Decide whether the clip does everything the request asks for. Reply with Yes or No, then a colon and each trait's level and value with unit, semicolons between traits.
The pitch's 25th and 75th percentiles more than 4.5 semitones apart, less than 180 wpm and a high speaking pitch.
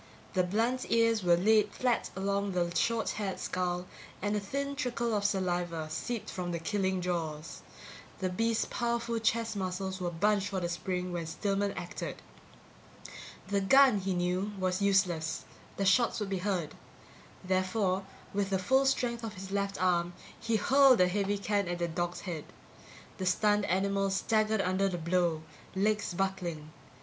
No: average, 2.9 semitones; average, 160 wpm; high, 195 Hz